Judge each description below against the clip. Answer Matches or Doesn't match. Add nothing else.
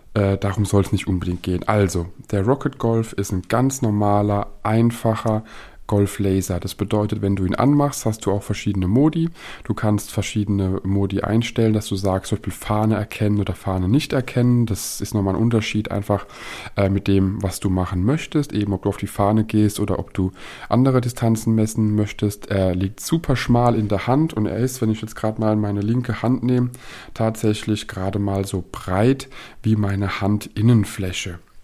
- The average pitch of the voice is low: Matches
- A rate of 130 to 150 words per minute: Doesn't match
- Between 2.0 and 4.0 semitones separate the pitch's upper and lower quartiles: Matches